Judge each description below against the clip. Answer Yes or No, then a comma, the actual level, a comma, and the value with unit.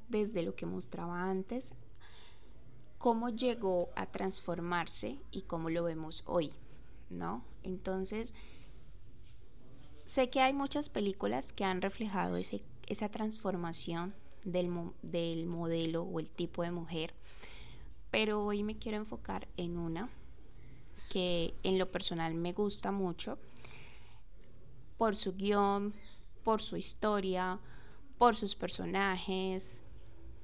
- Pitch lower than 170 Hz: No, medium, 185 Hz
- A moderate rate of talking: No, slow, 115 wpm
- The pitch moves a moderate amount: Yes, average, 3.5 semitones